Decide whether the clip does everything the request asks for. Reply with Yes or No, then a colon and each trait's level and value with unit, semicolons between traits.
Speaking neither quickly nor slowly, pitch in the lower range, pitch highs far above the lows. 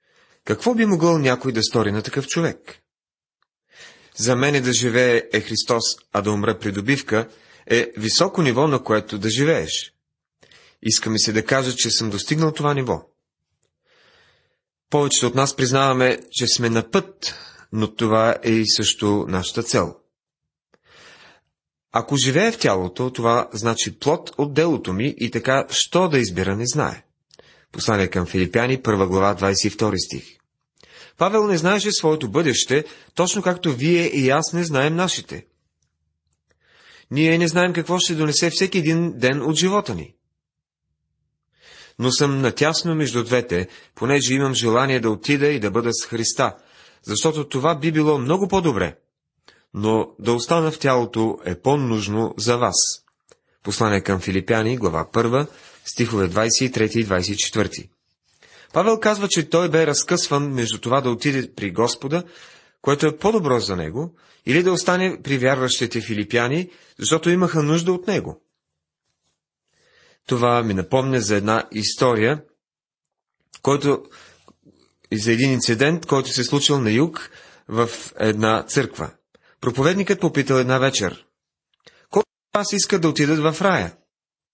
Yes: average, 140 wpm; low, 130 Hz; wide, 6.1 semitones